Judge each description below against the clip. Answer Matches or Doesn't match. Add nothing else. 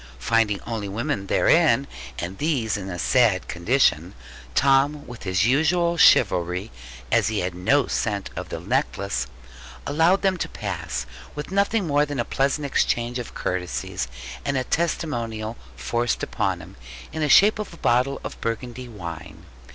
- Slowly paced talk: Doesn't match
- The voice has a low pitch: Matches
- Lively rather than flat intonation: Matches